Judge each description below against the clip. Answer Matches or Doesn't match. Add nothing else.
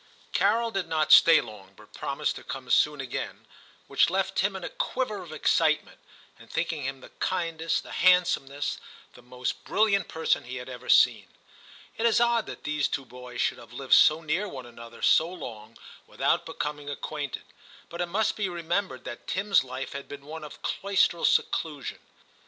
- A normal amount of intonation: Doesn't match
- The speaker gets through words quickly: Doesn't match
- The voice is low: Doesn't match